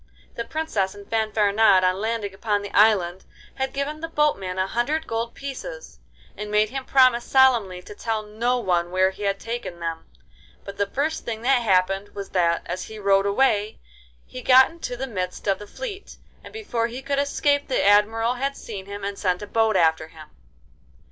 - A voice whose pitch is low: No, high, 215 Hz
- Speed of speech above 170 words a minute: Yes, average, 190 wpm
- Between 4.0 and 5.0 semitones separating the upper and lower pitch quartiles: Yes, average, 4.7 semitones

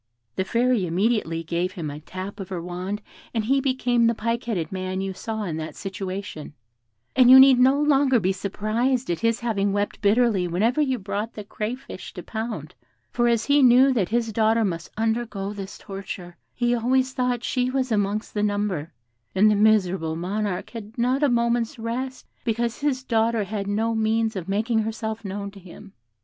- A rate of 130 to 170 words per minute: No, average, 185 wpm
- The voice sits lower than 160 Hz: No, high, 220 Hz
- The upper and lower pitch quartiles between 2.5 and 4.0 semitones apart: Yes, average, 3.7 semitones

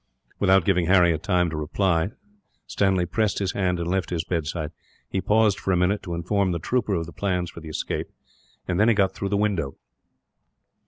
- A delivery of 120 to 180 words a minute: No, average, 200 wpm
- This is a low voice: Yes, very low, 90 Hz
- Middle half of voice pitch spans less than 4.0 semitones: Yes, average, 2.7 semitones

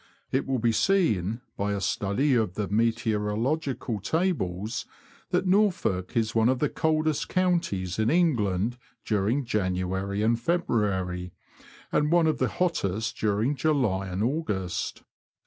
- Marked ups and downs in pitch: Yes, wide, 7.0 semitones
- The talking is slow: Yes, slow, 130 wpm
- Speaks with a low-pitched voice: Yes, low, 115 Hz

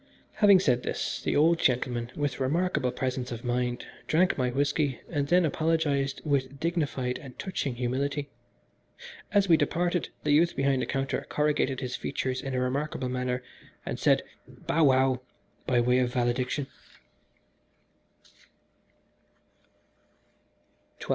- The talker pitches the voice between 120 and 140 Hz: Yes, low, 135 Hz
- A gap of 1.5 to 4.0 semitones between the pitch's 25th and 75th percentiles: Yes, average, 3.2 semitones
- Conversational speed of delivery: No, slow, 130 wpm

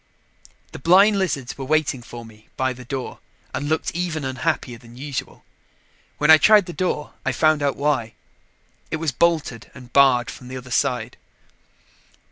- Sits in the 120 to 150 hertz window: Yes, medium, 140 Hz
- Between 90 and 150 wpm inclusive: No, average, 165 wpm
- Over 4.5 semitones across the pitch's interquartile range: No, average, 4.0 semitones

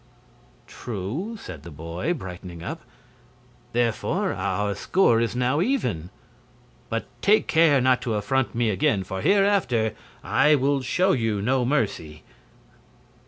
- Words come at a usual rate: No, slow, 125 wpm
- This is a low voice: Yes, low, 120 Hz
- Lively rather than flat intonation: Yes, wide, 7.0 semitones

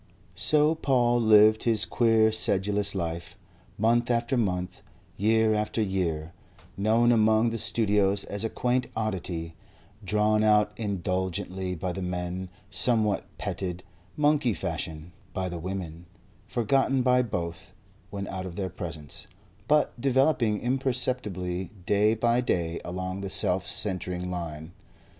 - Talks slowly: Yes, slow, 125 wpm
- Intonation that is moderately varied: Yes, average, 4.1 semitones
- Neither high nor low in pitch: No, low, 100 Hz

